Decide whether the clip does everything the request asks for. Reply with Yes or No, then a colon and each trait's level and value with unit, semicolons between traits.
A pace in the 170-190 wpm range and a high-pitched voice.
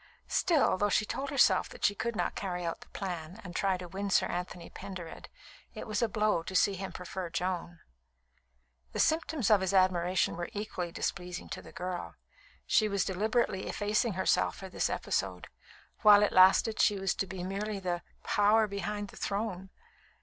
Yes: average, 180 wpm; high, 195 Hz